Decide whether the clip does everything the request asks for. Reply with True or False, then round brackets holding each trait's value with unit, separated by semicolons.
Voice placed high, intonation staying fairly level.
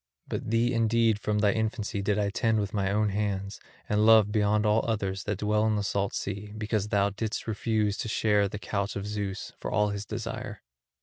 False (105 Hz; 1.3 semitones)